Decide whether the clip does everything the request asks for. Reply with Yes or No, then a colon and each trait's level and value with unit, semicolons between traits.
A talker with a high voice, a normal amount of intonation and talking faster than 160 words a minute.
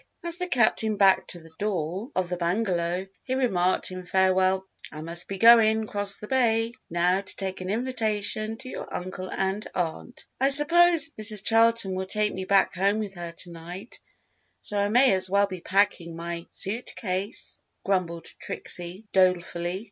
Yes: high, 195 Hz; average, 3.5 semitones; average, 170 wpm